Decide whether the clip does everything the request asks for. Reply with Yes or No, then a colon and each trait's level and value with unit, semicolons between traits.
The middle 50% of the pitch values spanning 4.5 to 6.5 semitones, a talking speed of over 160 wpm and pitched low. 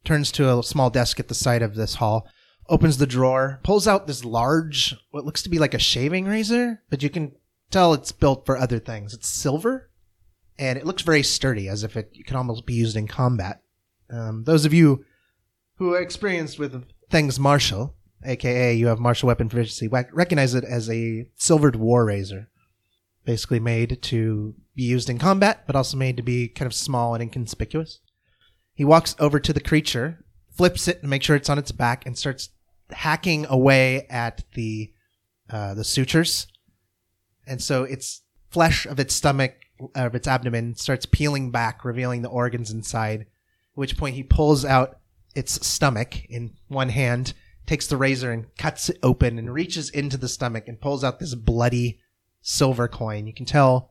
No: average, 4.1 semitones; average, 185 wpm; low, 125 Hz